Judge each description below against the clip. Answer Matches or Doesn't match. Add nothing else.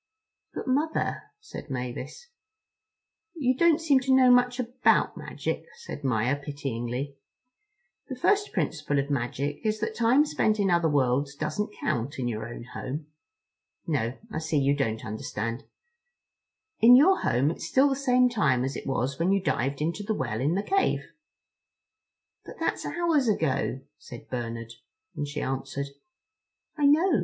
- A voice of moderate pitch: Matches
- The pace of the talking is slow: Doesn't match